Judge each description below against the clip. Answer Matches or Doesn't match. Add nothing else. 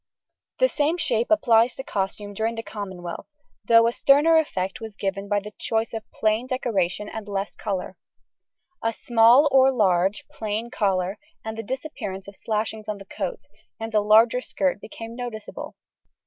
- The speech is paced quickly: Doesn't match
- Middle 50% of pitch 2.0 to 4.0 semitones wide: Matches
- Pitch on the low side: Doesn't match